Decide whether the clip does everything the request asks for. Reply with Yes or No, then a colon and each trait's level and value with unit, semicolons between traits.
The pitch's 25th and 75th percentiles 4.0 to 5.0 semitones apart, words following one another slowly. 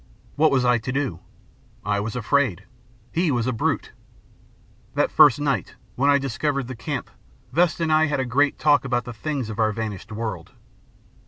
No: average, 4.3 semitones; average, 175 wpm